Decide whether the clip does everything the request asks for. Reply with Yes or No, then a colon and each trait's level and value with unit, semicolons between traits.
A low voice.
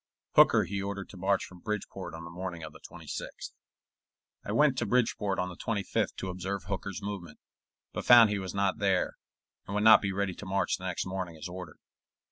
Yes: very low, 95 Hz